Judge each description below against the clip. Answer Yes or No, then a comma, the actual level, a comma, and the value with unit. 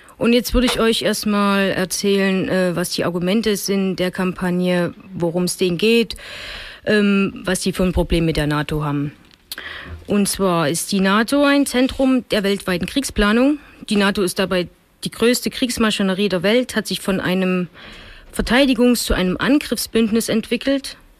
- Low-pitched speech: No, high, 200 Hz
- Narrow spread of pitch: No, average, 4.1 semitones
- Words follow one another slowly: No, average, 155 wpm